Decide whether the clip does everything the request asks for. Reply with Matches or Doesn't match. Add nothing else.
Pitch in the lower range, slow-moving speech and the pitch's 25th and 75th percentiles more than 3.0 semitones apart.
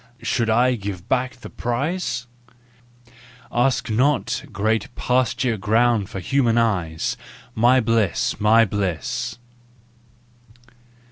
Doesn't match